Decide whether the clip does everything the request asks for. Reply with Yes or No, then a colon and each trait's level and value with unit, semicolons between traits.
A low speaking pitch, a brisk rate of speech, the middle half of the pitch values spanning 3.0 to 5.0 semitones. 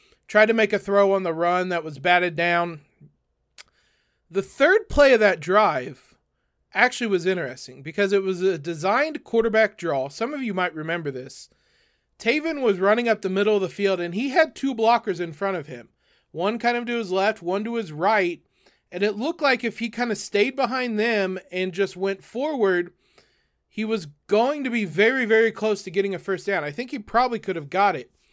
No: high, 200 Hz; fast, 210 wpm; average, 4.2 semitones